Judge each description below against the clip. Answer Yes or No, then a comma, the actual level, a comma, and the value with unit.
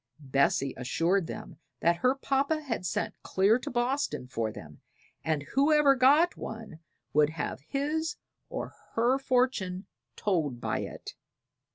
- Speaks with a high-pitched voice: Yes, high, 220 Hz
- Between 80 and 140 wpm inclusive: Yes, slow, 135 wpm